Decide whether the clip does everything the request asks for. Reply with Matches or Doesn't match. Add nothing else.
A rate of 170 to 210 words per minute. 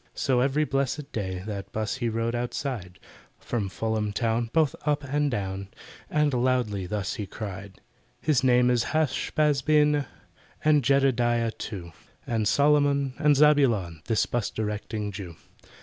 Doesn't match